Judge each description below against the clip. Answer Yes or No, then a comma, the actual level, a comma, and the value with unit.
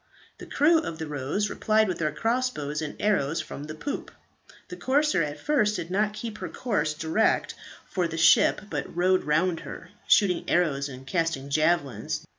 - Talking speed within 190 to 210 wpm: No, average, 175 wpm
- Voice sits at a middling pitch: Yes, medium, 170 Hz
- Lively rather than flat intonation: Yes, wide, 5.9 semitones